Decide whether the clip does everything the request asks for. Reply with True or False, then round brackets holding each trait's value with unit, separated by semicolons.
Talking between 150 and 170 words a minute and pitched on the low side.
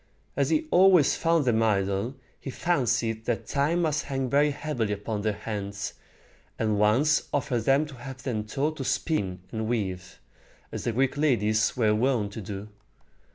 True (160 wpm; 120 Hz)